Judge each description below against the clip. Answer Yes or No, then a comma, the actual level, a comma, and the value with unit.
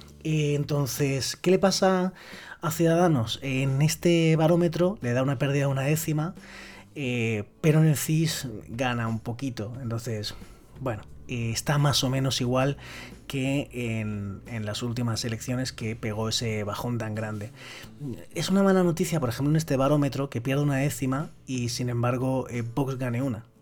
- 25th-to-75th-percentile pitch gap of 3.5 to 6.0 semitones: Yes, average, 4.8 semitones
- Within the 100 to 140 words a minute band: No, average, 165 wpm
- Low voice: Yes, low, 130 Hz